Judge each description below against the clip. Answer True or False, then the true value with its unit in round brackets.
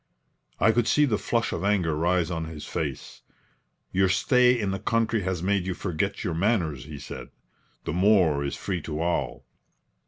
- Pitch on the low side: True (90 Hz)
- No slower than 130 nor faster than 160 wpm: False (180 wpm)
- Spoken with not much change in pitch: False (4.3 semitones)